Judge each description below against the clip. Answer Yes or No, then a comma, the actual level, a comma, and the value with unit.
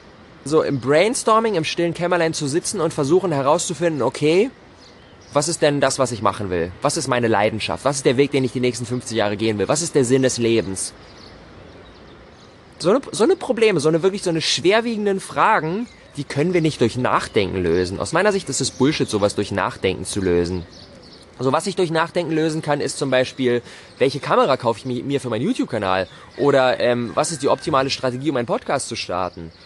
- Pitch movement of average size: No, wide, 7.6 semitones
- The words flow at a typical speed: No, fast, 205 wpm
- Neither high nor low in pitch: No, low, 130 Hz